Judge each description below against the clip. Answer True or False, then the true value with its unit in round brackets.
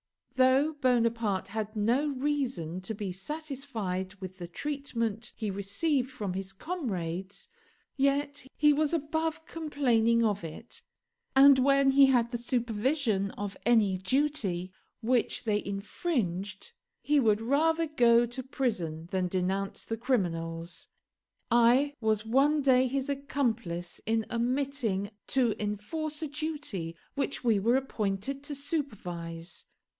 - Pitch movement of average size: False (6.0 semitones)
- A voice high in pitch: True (235 Hz)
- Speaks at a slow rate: True (125 wpm)